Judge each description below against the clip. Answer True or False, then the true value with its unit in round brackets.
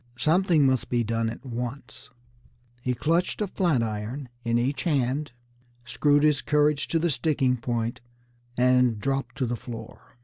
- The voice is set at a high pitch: False (130 Hz)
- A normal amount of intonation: True (3.8 semitones)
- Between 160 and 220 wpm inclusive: False (150 wpm)